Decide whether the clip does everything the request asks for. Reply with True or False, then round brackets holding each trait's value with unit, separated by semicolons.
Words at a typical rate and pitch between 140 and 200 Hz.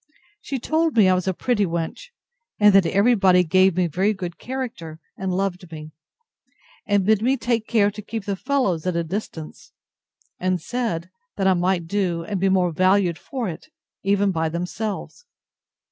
True (180 wpm; 190 Hz)